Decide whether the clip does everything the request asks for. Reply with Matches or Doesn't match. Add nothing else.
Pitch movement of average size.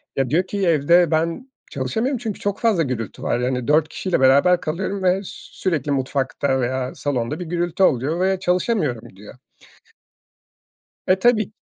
Doesn't match